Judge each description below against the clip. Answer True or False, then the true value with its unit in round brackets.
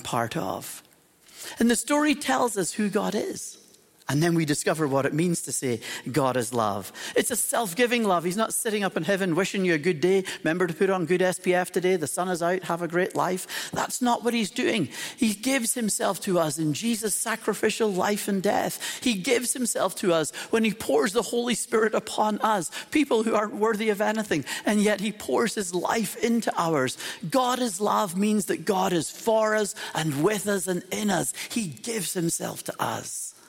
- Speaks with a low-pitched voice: False (205 Hz)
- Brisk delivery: True (210 wpm)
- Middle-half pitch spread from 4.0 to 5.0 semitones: True (4.3 semitones)